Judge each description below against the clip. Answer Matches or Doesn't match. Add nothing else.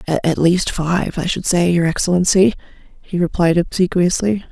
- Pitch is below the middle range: Doesn't match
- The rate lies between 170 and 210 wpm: Doesn't match